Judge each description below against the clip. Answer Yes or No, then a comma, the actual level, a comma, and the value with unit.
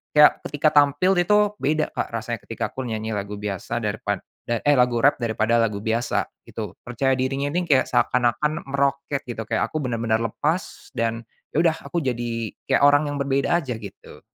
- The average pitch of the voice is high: No, low, 125 Hz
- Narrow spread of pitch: No, average, 4.1 semitones